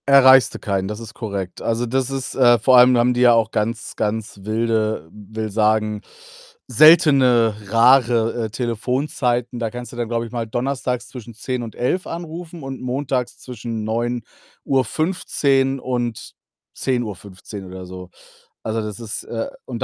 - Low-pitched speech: Yes, low, 120 Hz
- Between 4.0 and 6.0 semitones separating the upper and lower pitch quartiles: No, average, 2.8 semitones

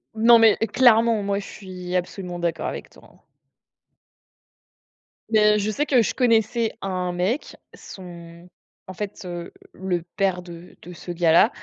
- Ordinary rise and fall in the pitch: Yes, average, 3.9 semitones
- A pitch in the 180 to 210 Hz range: Yes, high, 190 Hz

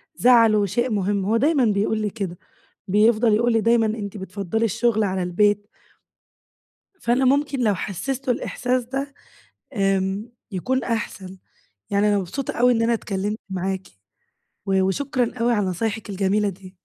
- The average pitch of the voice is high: Yes, high, 215 Hz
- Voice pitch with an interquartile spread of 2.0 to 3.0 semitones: No, average, 3.5 semitones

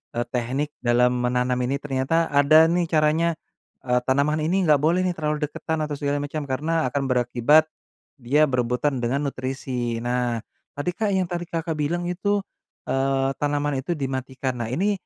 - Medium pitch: Yes, medium, 145 Hz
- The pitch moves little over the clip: No, average, 3.8 semitones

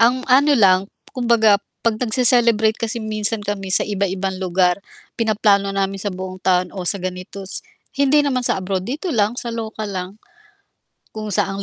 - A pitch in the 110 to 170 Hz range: No, high, 205 Hz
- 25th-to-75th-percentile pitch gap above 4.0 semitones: No, average, 3.4 semitones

